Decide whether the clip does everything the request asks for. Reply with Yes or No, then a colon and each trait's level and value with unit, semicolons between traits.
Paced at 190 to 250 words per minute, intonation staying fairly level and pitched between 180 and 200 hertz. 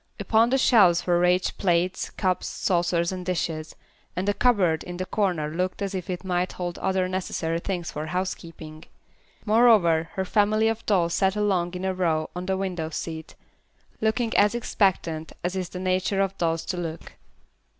No: average, 175 wpm; narrow, 2.3 semitones; medium, 185 Hz